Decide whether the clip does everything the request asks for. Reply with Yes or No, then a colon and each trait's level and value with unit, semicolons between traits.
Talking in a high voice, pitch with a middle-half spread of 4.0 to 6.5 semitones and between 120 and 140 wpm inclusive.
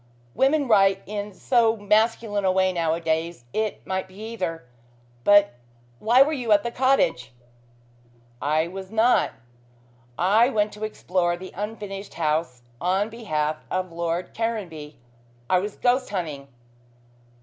Yes: high, 195 Hz; average, 4.8 semitones; slow, 135 wpm